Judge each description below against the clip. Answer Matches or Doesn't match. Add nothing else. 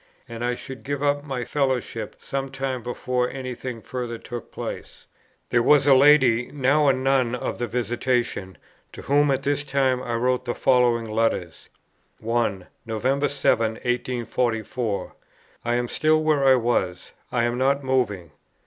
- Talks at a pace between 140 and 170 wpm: Matches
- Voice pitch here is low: Matches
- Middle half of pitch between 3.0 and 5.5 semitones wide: Doesn't match